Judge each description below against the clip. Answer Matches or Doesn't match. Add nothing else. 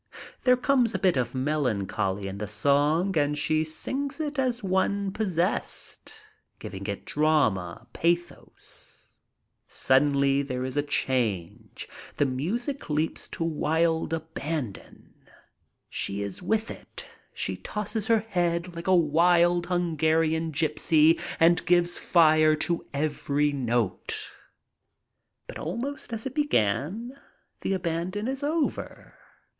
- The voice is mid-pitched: Matches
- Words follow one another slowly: Matches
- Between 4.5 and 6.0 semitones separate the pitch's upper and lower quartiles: Matches